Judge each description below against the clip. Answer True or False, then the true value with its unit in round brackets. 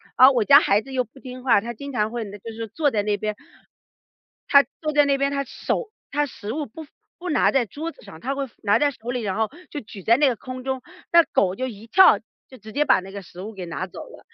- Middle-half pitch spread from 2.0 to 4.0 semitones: False (4.9 semitones)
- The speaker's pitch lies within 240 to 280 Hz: True (250 Hz)